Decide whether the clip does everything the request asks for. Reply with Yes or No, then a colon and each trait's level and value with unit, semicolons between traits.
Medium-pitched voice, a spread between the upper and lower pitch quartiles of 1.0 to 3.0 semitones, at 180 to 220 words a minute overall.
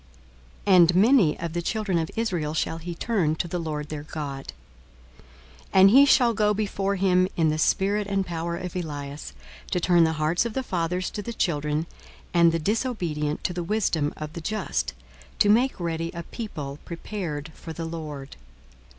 No: medium, 170 Hz; average, 4.4 semitones; average, 185 wpm